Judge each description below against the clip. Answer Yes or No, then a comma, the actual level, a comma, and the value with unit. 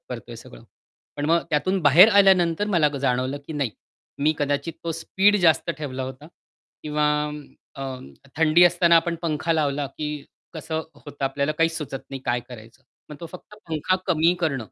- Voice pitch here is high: No, medium, 155 Hz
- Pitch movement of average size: Yes, average, 3.2 semitones